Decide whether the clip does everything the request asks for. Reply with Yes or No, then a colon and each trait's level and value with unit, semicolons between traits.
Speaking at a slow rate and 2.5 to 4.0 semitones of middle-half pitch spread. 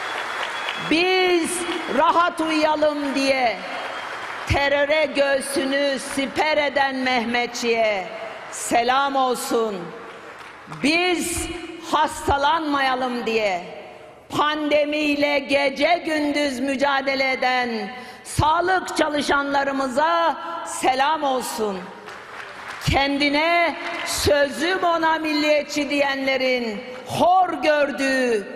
Yes: slow, 65 wpm; average, 3.4 semitones